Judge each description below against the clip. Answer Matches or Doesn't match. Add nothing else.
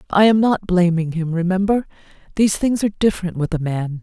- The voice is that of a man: Doesn't match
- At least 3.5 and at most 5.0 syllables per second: Doesn't match